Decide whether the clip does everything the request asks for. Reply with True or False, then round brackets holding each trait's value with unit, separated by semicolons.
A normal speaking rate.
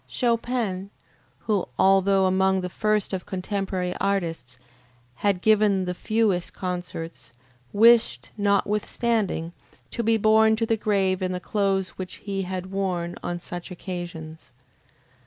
False (125 wpm)